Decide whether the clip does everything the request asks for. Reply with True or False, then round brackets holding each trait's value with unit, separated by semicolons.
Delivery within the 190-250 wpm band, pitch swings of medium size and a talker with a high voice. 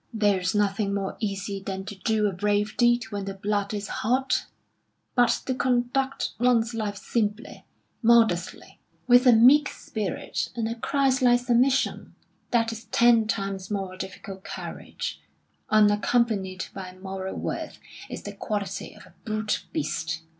False (145 wpm; 3.4 semitones; 215 Hz)